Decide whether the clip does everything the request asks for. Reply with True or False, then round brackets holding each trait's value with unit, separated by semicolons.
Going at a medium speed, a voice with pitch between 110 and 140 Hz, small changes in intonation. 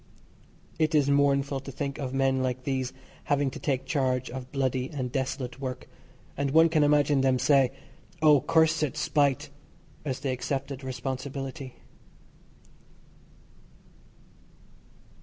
False (120 wpm; 135 Hz; 1.7 semitones)